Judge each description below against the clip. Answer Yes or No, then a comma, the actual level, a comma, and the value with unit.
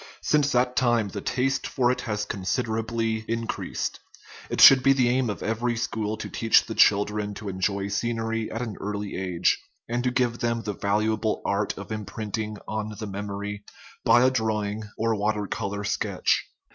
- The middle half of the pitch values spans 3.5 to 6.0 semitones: No, narrow, 2.4 semitones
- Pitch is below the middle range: Yes, low, 110 Hz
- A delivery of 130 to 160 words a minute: No, average, 170 wpm